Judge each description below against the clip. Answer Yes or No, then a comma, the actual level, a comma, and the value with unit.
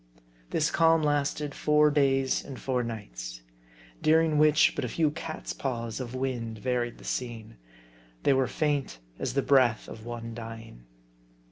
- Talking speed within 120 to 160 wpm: Yes, average, 150 wpm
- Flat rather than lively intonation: No, average, 4.3 semitones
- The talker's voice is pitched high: No, low, 130 Hz